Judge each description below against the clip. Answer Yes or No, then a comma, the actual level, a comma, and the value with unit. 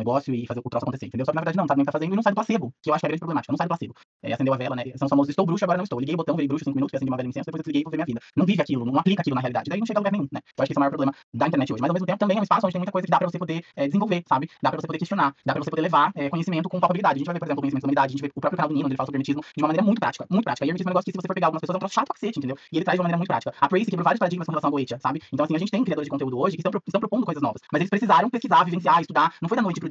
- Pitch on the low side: No, medium, 160 Hz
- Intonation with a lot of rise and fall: No, average, 4.7 semitones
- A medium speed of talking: No, fast, 355 wpm